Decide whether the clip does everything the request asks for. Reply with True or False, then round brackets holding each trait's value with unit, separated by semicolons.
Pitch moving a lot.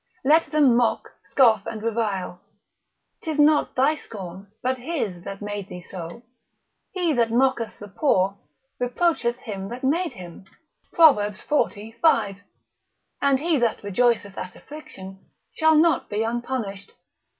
True (6.4 semitones)